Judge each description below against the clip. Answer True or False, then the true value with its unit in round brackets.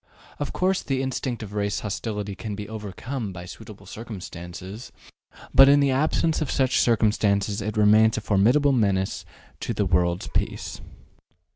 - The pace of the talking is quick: False (150 wpm)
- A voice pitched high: False (110 Hz)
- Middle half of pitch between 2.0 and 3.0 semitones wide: False (4.6 semitones)